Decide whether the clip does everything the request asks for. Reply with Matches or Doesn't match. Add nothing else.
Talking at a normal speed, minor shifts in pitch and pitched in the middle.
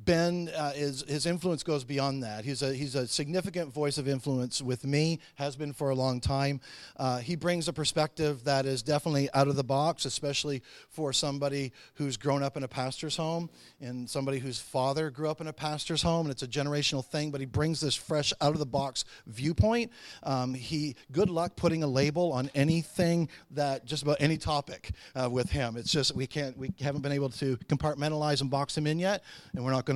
Doesn't match